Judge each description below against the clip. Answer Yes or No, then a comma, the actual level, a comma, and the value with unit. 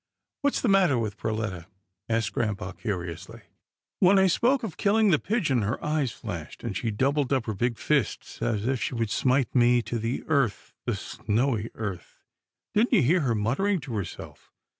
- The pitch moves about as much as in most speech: No, wide, 6.2 semitones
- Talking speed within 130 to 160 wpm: No, average, 185 wpm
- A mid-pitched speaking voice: No, low, 120 Hz